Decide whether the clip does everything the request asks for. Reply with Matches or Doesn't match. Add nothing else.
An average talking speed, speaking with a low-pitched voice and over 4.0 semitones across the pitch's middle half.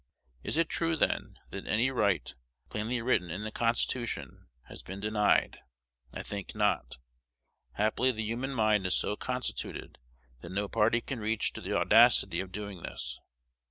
Doesn't match